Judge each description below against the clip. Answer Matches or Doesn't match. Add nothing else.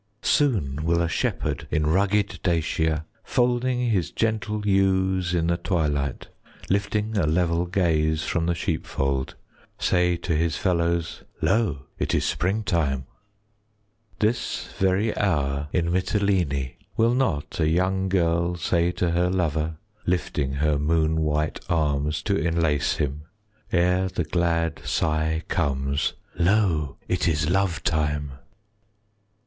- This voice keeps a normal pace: Doesn't match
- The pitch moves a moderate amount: Matches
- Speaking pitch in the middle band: Doesn't match